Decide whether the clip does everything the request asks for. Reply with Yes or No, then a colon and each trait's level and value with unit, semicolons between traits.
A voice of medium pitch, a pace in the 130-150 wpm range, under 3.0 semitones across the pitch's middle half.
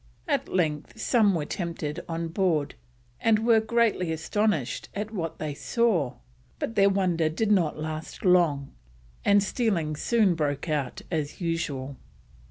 No: medium, 170 Hz; average, 140 wpm; average, 5.2 semitones